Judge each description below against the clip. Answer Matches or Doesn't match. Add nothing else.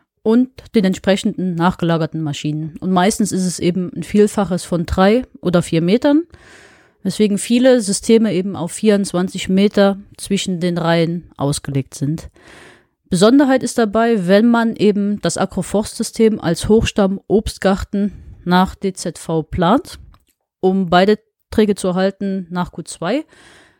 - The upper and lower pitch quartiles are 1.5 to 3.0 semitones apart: Doesn't match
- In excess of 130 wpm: Doesn't match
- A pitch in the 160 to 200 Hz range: Matches